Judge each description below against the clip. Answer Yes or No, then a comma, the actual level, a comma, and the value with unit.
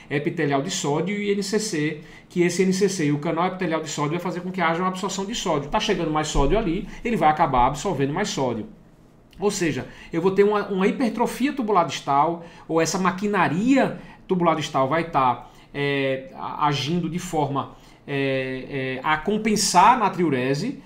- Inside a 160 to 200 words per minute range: Yes, average, 180 wpm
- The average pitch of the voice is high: No, medium, 165 Hz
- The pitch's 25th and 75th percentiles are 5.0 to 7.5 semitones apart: Yes, average, 5.3 semitones